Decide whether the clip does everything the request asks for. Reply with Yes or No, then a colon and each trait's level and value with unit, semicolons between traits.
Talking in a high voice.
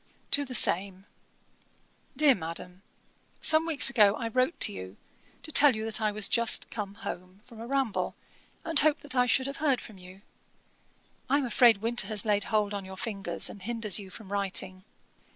Yes: high, 220 Hz